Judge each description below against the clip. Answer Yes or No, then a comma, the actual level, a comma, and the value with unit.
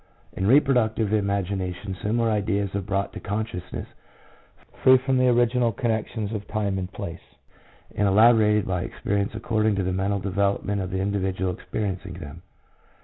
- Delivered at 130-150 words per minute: Yes, average, 145 wpm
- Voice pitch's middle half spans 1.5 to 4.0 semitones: Yes, narrow, 2.4 semitones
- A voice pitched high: No, low, 100 Hz